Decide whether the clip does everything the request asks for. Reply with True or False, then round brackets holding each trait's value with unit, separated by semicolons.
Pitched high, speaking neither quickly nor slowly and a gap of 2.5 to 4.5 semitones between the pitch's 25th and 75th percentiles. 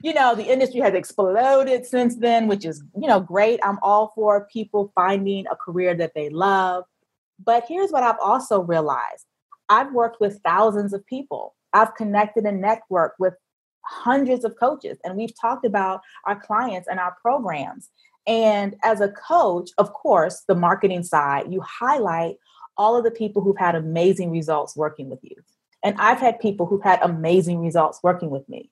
True (205 Hz; 180 wpm; 4.2 semitones)